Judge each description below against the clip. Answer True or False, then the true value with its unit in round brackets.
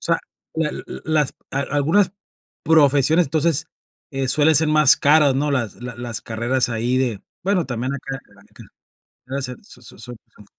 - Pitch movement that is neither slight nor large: True (3.8 semitones)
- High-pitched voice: False (135 Hz)